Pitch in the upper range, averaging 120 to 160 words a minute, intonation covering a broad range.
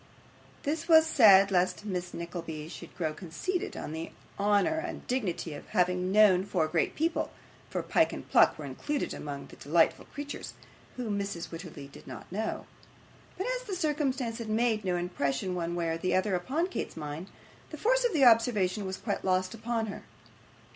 No: high, 195 Hz; average, 175 wpm; wide, 6.4 semitones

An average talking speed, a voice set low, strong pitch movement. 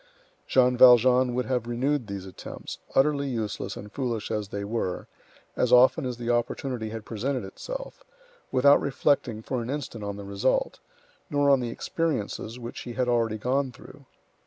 No: average, 165 wpm; low, 125 Hz; average, 3.3 semitones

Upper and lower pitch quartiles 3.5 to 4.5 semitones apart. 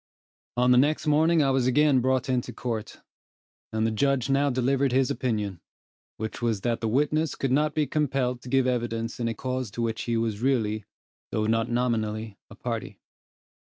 No: average, 3.1 semitones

